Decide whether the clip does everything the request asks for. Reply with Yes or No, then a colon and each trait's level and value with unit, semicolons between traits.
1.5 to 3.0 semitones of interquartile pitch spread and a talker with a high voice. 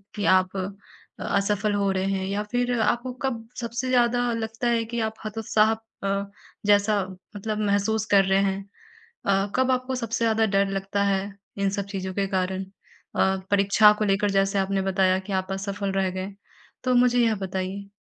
Yes: narrow, 2.5 semitones; high, 200 Hz